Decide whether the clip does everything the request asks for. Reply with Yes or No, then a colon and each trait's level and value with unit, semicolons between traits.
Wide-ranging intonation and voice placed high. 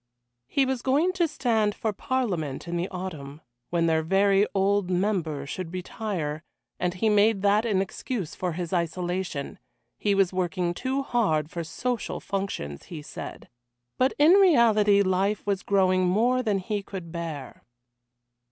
No: average, 4.0 semitones; high, 195 Hz